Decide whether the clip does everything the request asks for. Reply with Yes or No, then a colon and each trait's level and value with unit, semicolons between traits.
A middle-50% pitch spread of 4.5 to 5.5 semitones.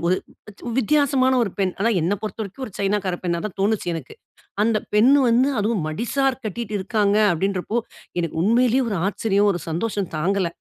No: average, 3.8 semitones